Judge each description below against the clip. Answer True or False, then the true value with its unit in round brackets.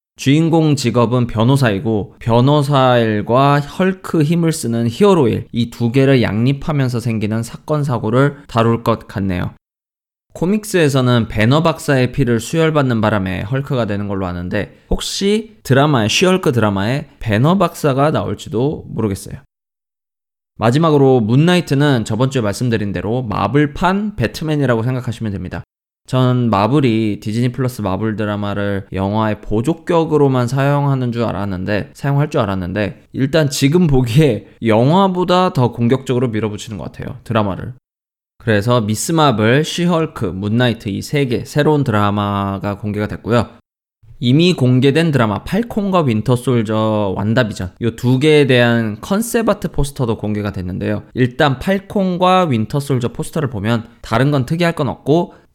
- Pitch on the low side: True (125 Hz)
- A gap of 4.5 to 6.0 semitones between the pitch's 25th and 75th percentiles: True (5.5 semitones)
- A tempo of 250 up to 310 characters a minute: False (340 characters per minute)